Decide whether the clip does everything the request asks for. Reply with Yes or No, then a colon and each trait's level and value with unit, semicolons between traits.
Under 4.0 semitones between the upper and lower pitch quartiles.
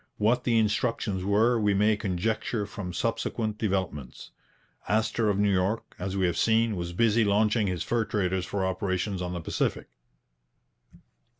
Yes: average, 3.1 semitones